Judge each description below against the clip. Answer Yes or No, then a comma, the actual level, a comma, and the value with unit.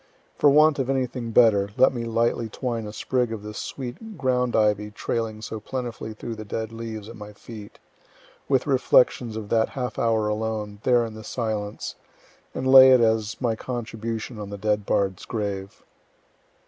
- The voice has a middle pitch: No, low, 115 Hz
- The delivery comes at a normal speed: Yes, average, 175 wpm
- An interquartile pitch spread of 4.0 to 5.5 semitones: No, average, 2.7 semitones